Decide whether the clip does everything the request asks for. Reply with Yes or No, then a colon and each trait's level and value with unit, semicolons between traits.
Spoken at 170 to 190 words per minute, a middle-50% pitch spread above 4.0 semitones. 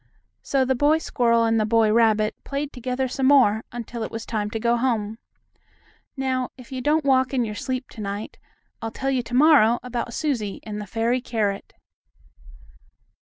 No: average, 180 wpm; average, 2.9 semitones